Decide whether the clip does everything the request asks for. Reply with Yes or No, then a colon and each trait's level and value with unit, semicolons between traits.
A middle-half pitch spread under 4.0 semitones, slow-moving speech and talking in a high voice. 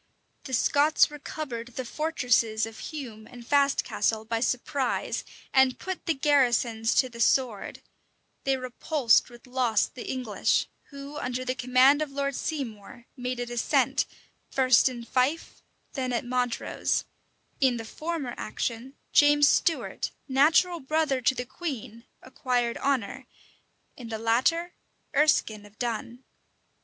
Yes: average, 3.1 semitones; slow, 130 wpm; very high, 255 Hz